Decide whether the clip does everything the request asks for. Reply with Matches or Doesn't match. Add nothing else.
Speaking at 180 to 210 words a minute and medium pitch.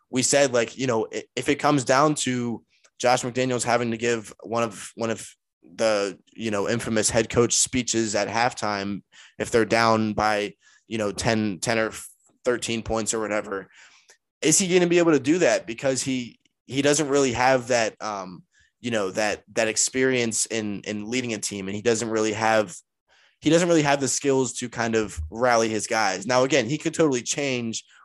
Doesn't match